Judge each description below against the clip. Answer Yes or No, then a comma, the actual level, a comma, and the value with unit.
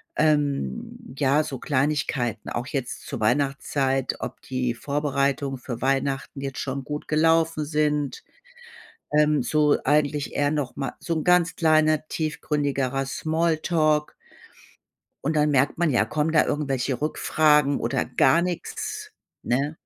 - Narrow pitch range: Yes, narrow, 2.3 semitones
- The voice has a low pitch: No, medium, 145 Hz